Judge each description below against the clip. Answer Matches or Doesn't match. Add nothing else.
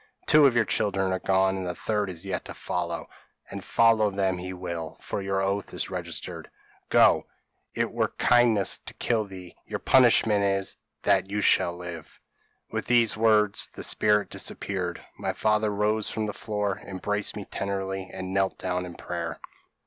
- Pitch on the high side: Doesn't match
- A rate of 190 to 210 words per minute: Doesn't match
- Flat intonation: Matches